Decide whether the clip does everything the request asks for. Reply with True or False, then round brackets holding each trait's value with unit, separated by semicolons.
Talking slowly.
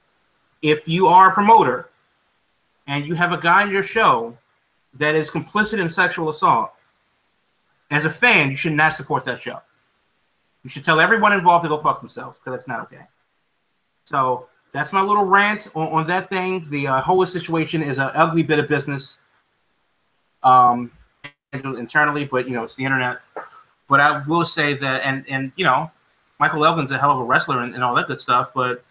False (190 wpm)